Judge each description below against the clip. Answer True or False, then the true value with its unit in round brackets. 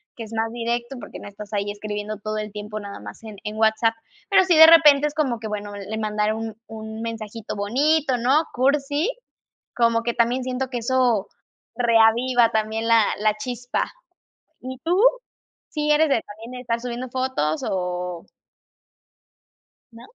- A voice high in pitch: True (230 Hz)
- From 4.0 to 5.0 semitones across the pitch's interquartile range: False (3.2 semitones)